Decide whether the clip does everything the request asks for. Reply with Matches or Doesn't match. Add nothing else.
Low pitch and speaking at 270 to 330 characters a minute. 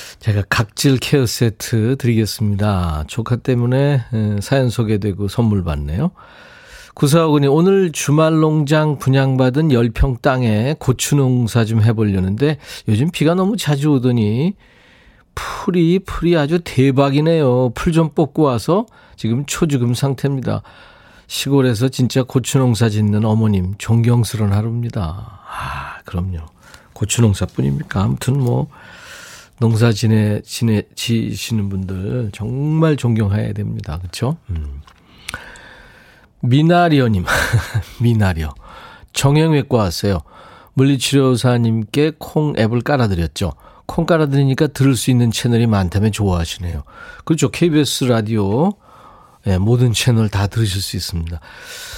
Matches